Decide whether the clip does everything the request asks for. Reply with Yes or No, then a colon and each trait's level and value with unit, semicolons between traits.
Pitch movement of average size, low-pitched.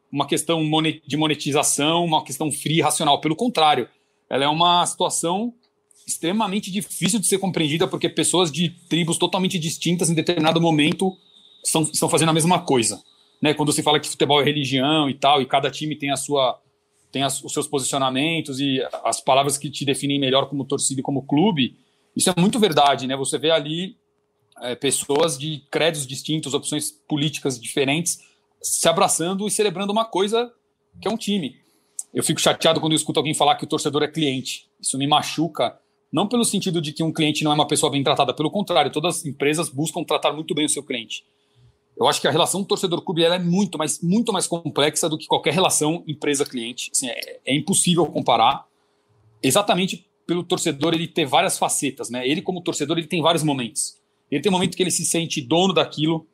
No: average, 3.4 semitones; medium, 155 Hz